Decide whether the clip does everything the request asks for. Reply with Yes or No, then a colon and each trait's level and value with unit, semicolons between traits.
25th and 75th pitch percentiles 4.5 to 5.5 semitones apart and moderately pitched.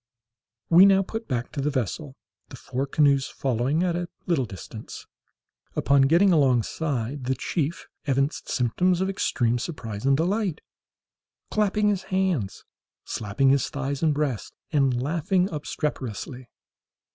Yes: average, 5.2 semitones; medium, 145 Hz